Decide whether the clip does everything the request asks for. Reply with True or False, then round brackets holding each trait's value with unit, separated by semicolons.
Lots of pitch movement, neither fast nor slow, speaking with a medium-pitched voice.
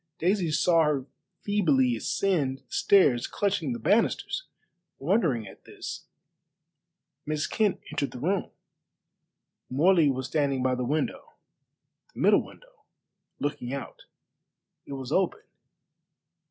False (6.2 semitones; 115 wpm; 150 Hz)